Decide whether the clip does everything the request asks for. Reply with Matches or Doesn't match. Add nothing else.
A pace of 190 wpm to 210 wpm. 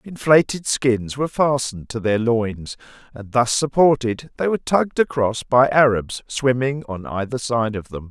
Doesn't match